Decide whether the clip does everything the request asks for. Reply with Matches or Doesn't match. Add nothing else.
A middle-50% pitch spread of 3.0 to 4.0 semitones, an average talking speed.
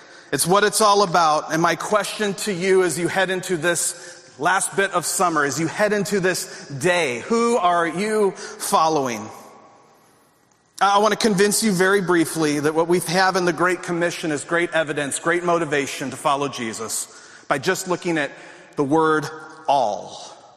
Matches